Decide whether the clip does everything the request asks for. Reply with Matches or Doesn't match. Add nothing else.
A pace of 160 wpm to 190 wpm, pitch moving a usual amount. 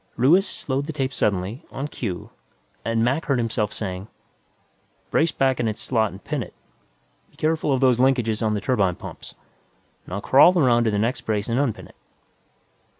Matches